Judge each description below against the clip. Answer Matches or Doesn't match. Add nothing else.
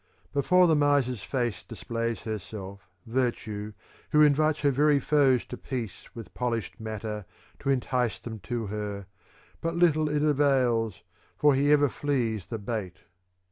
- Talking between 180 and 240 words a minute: Doesn't match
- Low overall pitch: Matches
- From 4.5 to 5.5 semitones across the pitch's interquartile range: Matches